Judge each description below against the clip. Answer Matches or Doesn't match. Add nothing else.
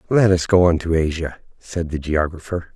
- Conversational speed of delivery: Matches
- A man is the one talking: Matches